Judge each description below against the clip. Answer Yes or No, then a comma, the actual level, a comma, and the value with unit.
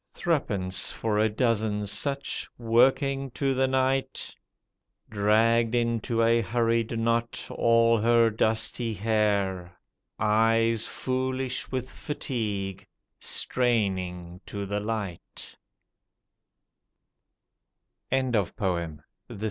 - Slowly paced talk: Yes, slow, 85 wpm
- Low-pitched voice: Yes, low, 115 Hz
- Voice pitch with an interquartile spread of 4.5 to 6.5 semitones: No, average, 2.7 semitones